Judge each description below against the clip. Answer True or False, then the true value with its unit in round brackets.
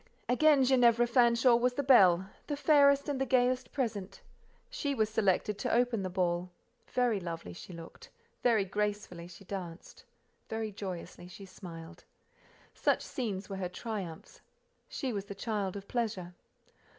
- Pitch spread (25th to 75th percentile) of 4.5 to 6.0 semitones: True (5.0 semitones)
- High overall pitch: True (210 Hz)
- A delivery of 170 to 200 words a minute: False (145 wpm)